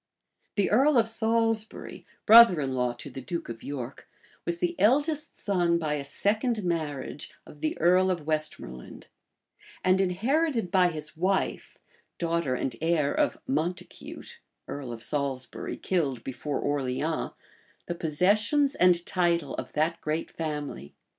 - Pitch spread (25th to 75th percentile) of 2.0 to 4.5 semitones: No, average, 5.2 semitones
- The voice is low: No, medium, 170 Hz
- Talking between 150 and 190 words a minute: No, average, 140 wpm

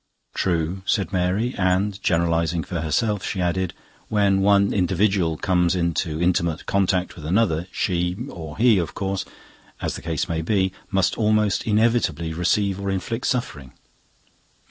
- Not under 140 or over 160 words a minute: Yes, average, 145 wpm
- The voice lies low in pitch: Yes, very low, 95 Hz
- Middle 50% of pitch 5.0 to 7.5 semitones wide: No, average, 3.0 semitones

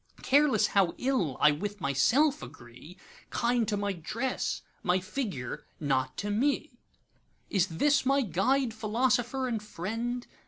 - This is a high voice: Yes, high, 215 Hz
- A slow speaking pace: Yes, slow, 115 wpm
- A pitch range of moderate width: No, wide, 6.5 semitones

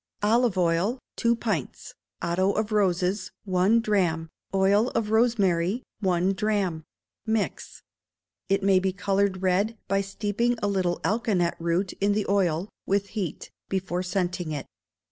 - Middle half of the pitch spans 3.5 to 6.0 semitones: No, average, 2.8 semitones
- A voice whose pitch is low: No, high, 195 Hz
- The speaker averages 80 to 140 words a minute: Yes, slow, 135 wpm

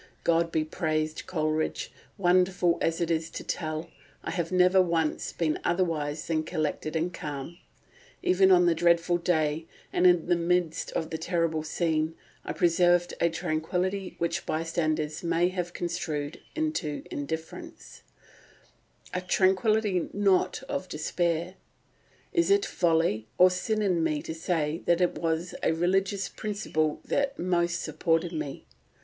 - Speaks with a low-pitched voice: No, medium, 170 Hz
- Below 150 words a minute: Yes, average, 140 wpm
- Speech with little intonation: Yes, narrow, 2.3 semitones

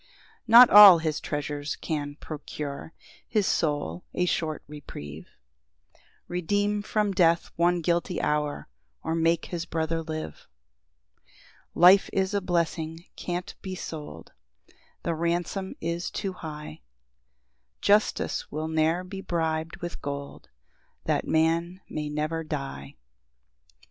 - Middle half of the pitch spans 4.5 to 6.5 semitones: No, average, 2.9 semitones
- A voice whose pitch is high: No, medium, 165 Hz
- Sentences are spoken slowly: Yes, slow, 125 wpm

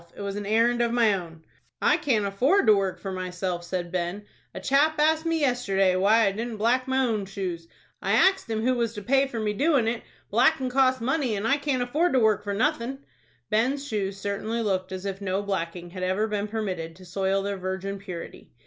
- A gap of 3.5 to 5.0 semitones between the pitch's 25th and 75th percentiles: Yes, average, 4.7 semitones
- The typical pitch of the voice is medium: No, high, 210 Hz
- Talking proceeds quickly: Yes, fast, 215 wpm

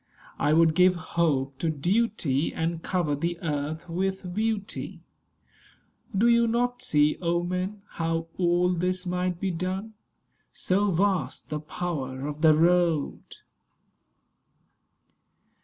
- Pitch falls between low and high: Yes, medium, 175 Hz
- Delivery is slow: Yes, slow, 120 wpm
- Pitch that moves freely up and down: No, average, 3.0 semitones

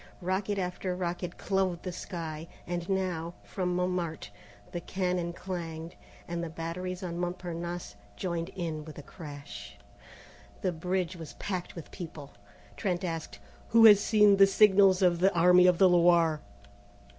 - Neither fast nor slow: Yes, average, 145 wpm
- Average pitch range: No, narrow, 1.9 semitones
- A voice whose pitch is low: No, medium, 175 Hz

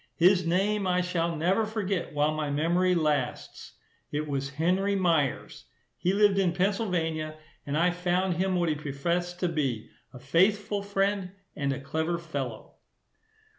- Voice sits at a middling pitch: Yes, medium, 175 Hz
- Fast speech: No, average, 150 wpm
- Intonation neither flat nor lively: Yes, average, 3.7 semitones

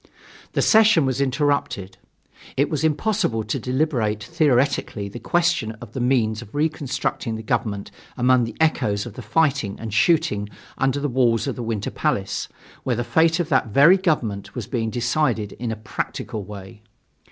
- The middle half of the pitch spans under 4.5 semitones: No, wide, 5.5 semitones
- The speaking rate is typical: Yes, average, 165 wpm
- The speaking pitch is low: Yes, low, 125 Hz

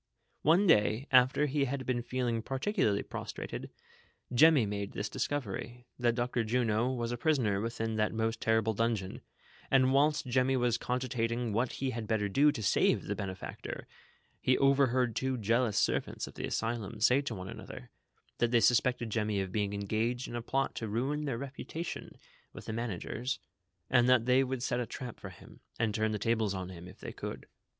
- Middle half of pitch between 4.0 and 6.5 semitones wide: No, average, 3.0 semitones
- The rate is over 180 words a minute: Yes, average, 190 wpm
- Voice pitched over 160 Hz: No, low, 120 Hz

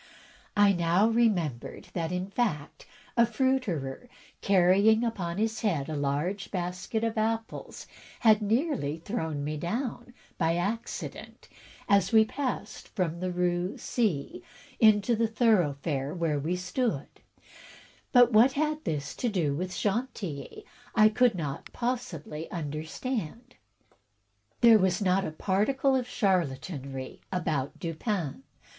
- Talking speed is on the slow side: Yes, slow, 125 wpm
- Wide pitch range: Yes, wide, 5.8 semitones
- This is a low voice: No, high, 190 Hz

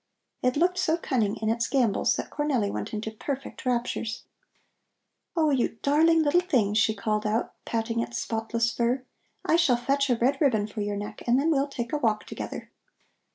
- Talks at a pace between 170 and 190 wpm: Yes, average, 185 wpm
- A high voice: Yes, high, 240 Hz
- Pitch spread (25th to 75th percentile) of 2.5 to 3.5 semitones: No, average, 4.3 semitones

